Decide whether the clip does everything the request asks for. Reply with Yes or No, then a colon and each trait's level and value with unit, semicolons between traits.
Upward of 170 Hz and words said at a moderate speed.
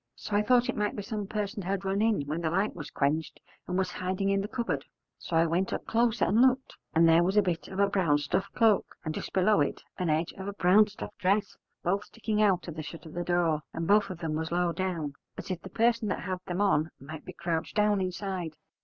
No: medium, 185 Hz; fast, 250 wpm